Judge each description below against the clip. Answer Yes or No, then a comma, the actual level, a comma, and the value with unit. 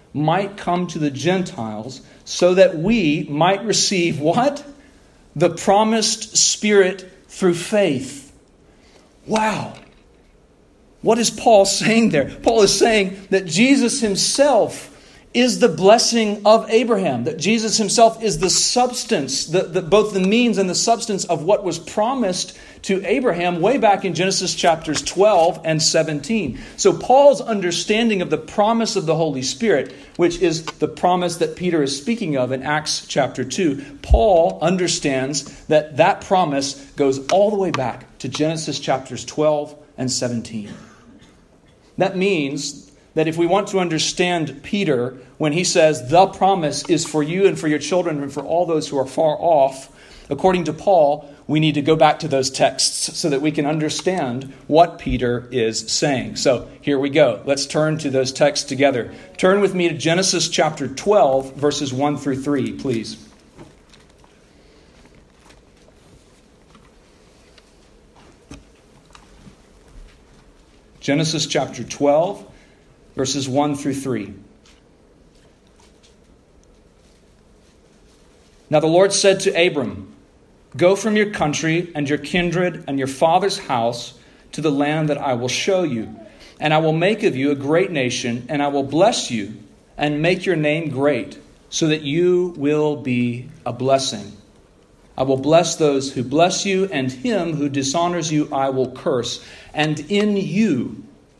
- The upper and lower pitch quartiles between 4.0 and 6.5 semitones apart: Yes, average, 5.2 semitones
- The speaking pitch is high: No, medium, 160 Hz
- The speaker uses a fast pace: No, average, 145 wpm